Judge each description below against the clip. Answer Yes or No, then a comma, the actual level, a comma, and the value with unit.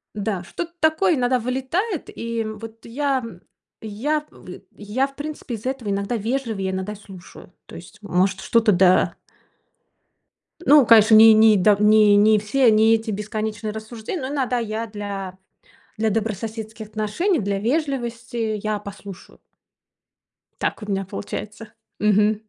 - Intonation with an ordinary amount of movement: Yes, average, 3.0 semitones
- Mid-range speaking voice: No, high, 220 Hz